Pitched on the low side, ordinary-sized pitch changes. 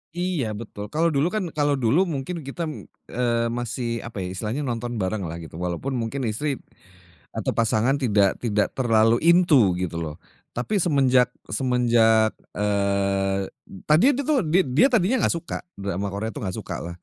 No: low, 120 Hz; wide, 6.1 semitones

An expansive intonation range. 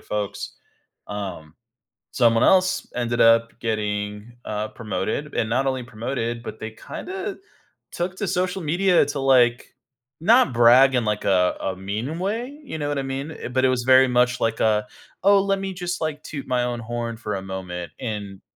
Yes: wide, 5.9 semitones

